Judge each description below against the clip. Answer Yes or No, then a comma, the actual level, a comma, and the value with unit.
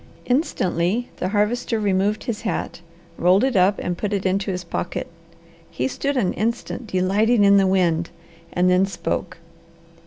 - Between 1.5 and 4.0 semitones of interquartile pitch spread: Yes, average, 3.3 semitones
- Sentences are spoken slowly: No, average, 155 wpm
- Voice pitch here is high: Yes, high, 195 Hz